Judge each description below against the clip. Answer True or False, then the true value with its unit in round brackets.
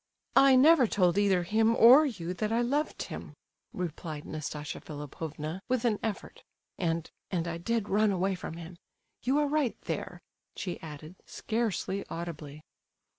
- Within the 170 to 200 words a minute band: False (140 wpm)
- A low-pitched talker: False (190 Hz)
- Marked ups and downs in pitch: True (5.9 semitones)